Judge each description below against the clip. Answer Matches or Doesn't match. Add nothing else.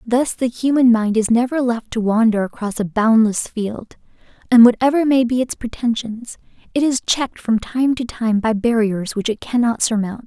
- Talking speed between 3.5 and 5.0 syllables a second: Matches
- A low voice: Doesn't match